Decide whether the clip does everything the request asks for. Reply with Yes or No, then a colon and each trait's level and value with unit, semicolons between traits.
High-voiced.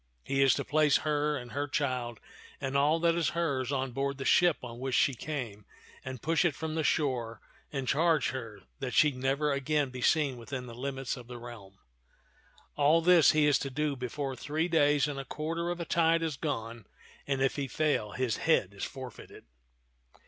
No: medium, 140 Hz